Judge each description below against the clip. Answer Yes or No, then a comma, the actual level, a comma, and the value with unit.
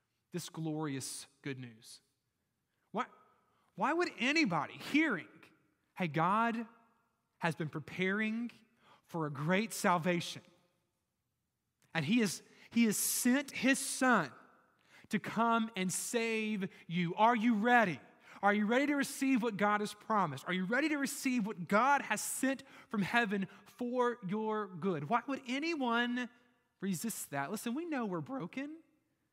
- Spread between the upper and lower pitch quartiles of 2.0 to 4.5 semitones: No, wide, 5.6 semitones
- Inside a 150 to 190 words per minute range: No, slow, 135 wpm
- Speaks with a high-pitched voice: Yes, high, 215 Hz